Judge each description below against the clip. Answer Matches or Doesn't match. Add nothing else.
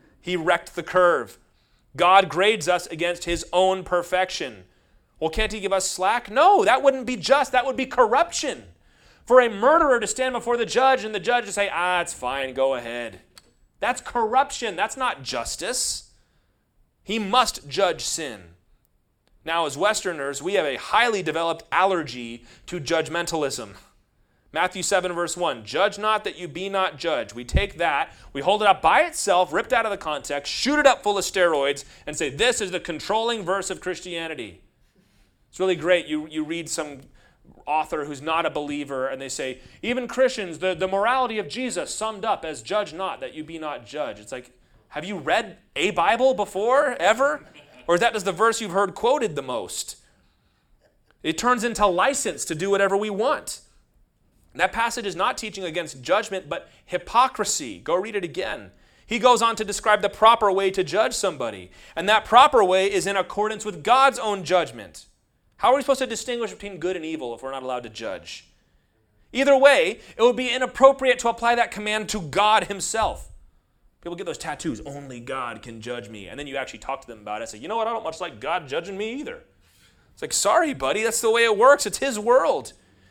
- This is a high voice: Matches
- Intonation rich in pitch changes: Matches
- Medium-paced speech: Matches